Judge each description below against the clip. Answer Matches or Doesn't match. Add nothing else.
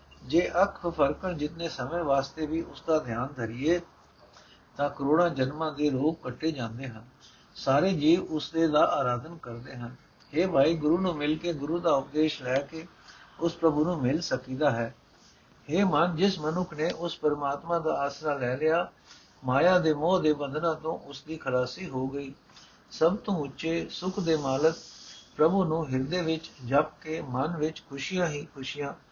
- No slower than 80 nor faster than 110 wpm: Doesn't match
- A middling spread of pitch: Matches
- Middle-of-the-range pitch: Matches